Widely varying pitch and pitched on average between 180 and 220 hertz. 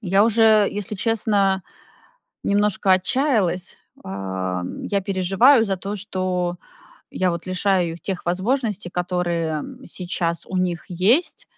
No: average, 2.9 semitones; medium, 185 Hz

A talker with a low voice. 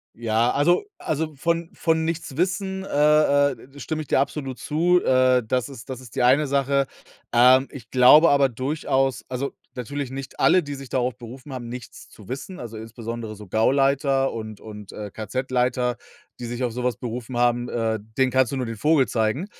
Yes: low, 130 Hz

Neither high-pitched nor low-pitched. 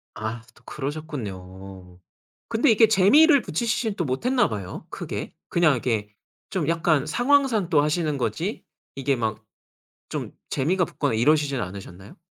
Yes: medium, 150 Hz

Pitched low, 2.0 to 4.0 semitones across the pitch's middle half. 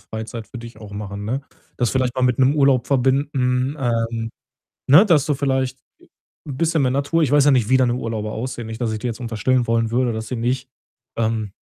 Yes: low, 125 Hz; average, 2.7 semitones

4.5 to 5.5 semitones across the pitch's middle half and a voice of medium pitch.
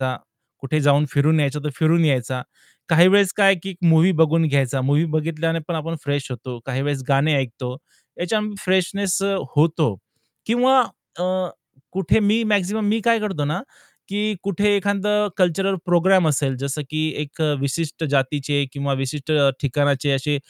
Yes: average, 5.2 semitones; medium, 155 Hz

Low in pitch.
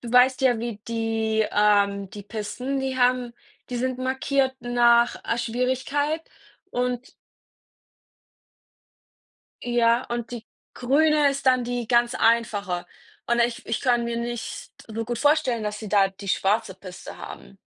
No: high, 240 Hz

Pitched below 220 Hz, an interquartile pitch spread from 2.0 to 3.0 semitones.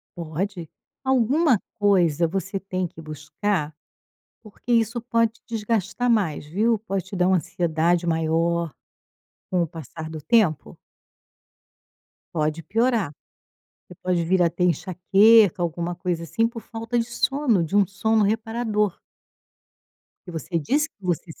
No: high, 190 Hz; average, 5.0 semitones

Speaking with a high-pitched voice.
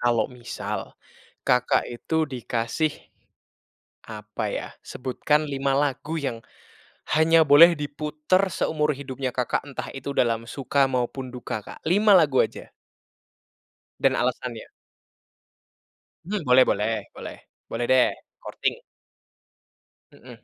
No: low, 135 Hz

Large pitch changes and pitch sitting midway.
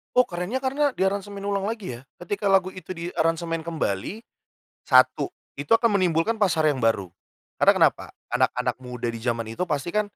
Yes: wide, 5.8 semitones; medium, 180 Hz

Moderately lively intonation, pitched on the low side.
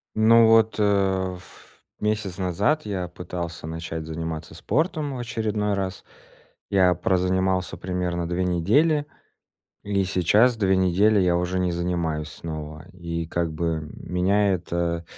Yes: average, 3.3 semitones; very low, 90 Hz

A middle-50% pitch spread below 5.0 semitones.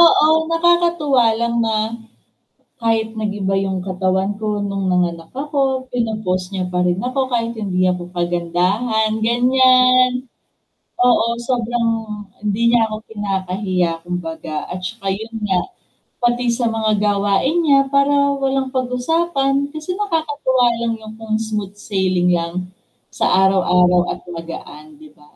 No: wide, 5.6 semitones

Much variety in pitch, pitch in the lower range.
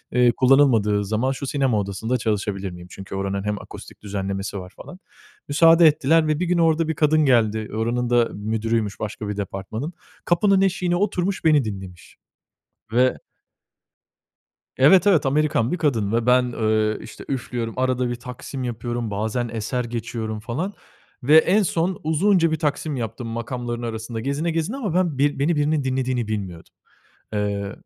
Yes: wide, 6.0 semitones; low, 125 Hz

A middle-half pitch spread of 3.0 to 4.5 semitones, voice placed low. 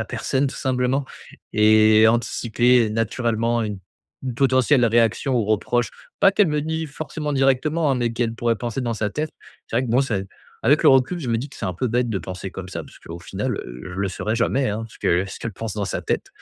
Yes: average, 3.7 semitones; low, 120 Hz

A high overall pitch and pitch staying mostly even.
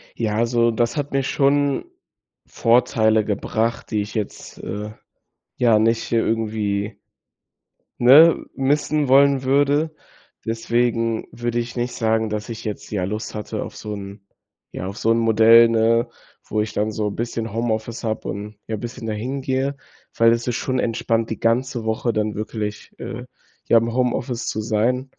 No: low, 115 Hz; narrow, 2.2 semitones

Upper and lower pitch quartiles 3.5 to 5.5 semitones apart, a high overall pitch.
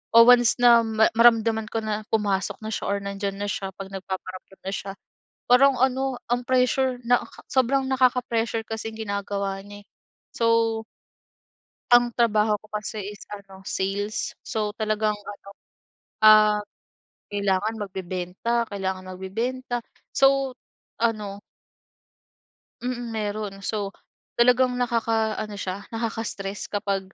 No: average, 3.0 semitones; high, 215 Hz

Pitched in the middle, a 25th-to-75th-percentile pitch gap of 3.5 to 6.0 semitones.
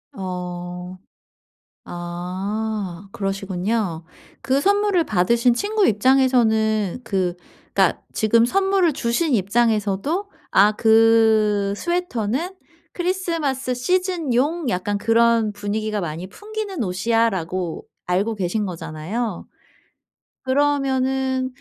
No: high, 225 Hz; wide, 5.5 semitones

